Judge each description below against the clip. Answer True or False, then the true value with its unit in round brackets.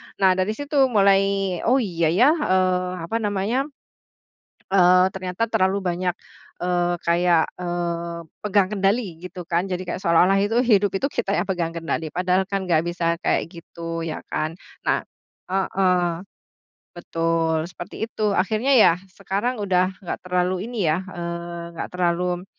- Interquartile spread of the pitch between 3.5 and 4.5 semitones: False (2.4 semitones)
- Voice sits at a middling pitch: True (180 Hz)